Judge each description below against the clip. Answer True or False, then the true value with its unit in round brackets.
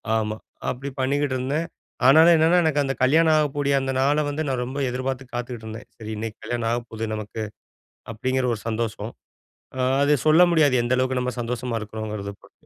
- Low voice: True (130 Hz)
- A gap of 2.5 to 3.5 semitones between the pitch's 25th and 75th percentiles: False (4.0 semitones)